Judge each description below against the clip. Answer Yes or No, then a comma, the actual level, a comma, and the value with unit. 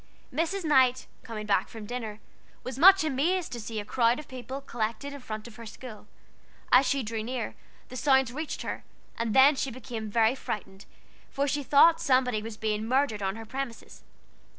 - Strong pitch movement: No, average, 3.8 semitones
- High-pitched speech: Yes, very high, 250 Hz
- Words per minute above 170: Yes, average, 185 wpm